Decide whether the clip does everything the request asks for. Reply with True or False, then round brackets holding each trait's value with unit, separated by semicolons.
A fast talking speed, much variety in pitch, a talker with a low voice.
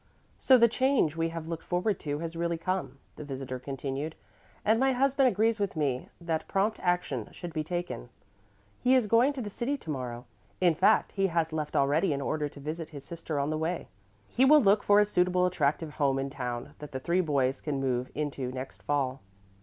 False (210 wpm; 5.7 semitones; 160 Hz)